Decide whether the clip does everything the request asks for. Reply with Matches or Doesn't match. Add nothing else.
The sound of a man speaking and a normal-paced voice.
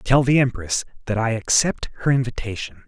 Matches